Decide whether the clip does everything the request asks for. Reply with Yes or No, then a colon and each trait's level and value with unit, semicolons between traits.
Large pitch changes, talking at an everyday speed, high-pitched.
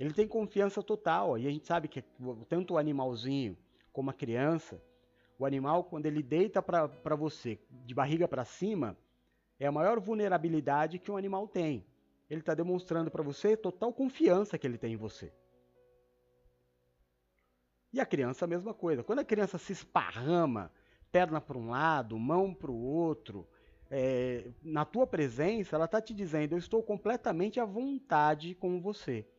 No: wide, 6.5 semitones; average, 165 wpm; medium, 155 Hz